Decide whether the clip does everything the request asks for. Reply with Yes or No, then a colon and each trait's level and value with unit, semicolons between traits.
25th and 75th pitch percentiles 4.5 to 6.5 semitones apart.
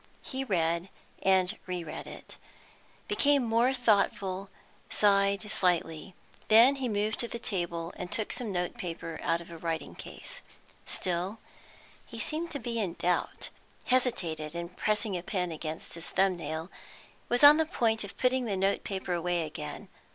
Yes: average, 5.1 semitones